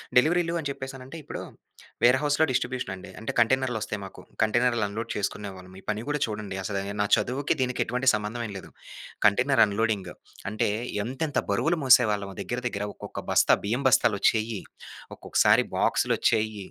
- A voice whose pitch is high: No, low, 115 Hz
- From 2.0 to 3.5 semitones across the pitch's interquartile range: No, average, 4.1 semitones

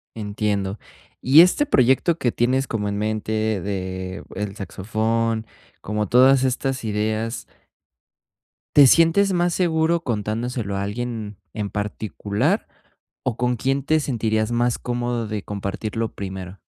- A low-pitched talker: Yes, low, 110 Hz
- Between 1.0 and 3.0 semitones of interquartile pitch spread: No, average, 3.8 semitones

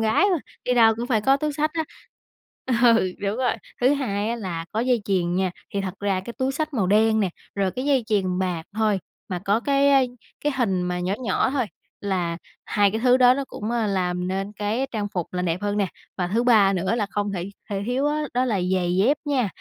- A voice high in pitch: Yes, high, 210 Hz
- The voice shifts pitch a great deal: No, average, 4.8 semitones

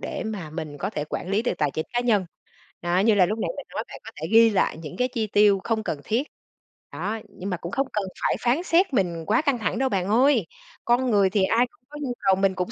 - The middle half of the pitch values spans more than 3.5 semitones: Yes, average, 4.6 semitones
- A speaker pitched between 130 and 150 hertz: No, high, 210 Hz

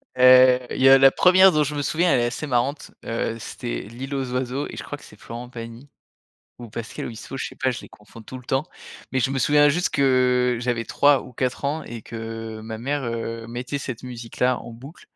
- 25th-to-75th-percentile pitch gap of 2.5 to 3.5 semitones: Yes, average, 2.8 semitones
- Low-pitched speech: Yes, low, 125 Hz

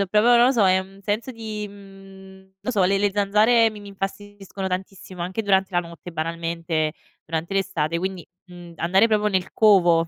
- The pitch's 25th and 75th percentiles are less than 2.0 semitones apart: No, narrow, 2.6 semitones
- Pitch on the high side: Yes, high, 195 Hz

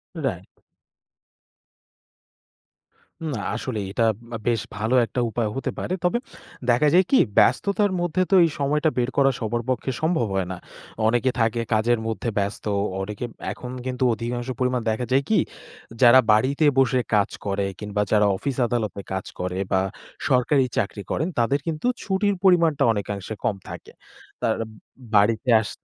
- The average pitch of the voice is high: No, low, 120 Hz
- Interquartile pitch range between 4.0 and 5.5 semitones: Yes, average, 4.5 semitones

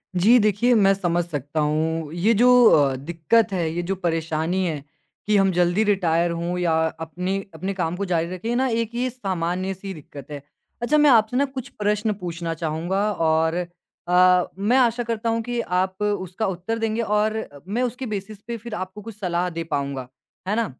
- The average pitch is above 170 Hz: Yes, high, 190 Hz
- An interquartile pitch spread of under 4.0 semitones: No, average, 4.8 semitones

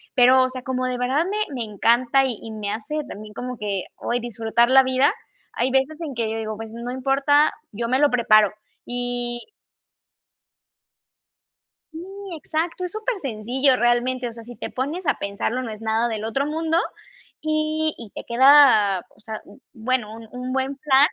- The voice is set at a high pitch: Yes, very high, 250 Hz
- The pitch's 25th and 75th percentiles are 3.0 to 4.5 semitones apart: Yes, average, 3.5 semitones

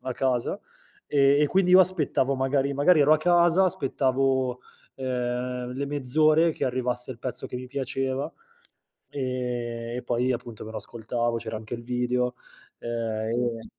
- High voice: No, low, 130 Hz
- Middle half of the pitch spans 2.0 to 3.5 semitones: Yes, narrow, 2.5 semitones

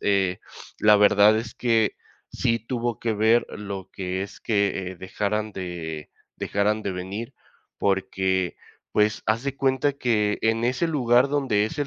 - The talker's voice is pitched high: No, low, 105 Hz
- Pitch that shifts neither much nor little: Yes, average, 3.3 semitones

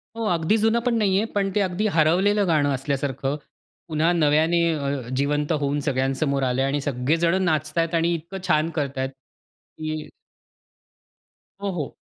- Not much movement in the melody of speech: No, average, 4.1 semitones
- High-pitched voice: No, medium, 155 Hz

